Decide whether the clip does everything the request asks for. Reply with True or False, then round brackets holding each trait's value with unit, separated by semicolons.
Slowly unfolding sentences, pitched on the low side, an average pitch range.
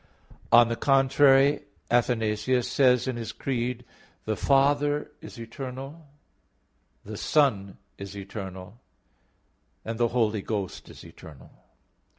True (105 wpm; 120 Hz; 4.1 semitones)